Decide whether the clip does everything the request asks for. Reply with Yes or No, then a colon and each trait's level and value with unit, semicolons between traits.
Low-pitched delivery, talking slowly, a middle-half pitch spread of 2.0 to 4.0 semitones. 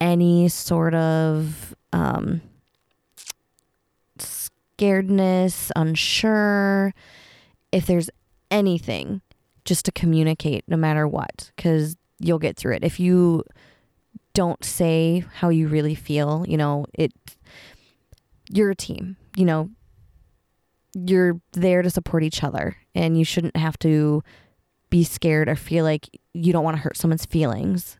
No: medium, 165 Hz; slow, 125 wpm; average, 2.7 semitones